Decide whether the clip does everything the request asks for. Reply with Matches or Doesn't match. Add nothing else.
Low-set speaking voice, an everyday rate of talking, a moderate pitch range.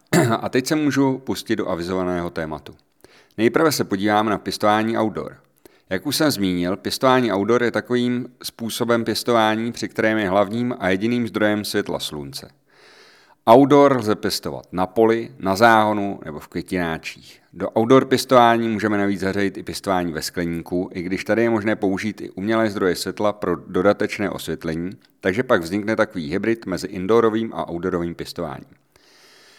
Matches